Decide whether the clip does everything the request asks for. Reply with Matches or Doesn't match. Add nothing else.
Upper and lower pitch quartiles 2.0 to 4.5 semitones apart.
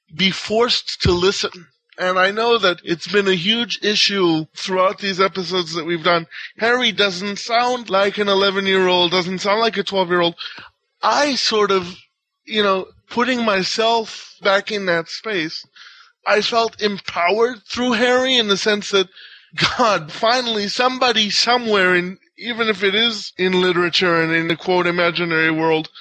Matches